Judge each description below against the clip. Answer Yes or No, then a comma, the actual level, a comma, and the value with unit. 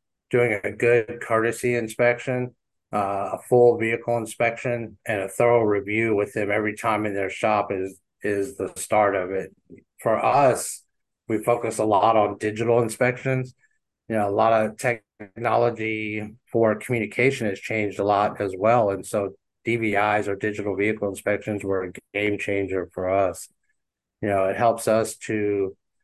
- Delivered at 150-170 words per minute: Yes, average, 160 wpm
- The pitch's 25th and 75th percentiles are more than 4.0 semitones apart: No, narrow, 2.6 semitones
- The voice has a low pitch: Yes, low, 110 Hz